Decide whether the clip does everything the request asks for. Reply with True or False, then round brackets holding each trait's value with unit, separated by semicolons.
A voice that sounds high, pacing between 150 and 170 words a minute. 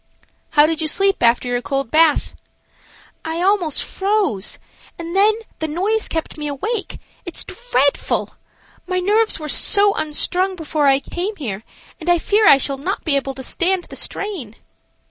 True (330 Hz; 165 wpm)